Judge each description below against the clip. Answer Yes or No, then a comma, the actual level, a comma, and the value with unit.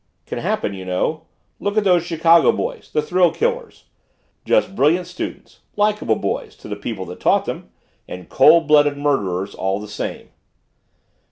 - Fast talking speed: No, average, 160 wpm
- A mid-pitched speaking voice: Yes, medium, 150 Hz